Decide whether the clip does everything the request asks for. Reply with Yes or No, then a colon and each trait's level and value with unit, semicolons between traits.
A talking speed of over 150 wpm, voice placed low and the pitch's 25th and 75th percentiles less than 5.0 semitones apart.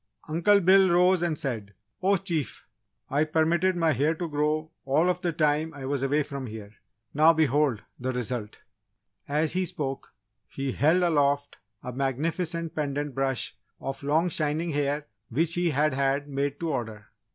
No: average, 165 wpm; medium, 150 Hz; average, 3.5 semitones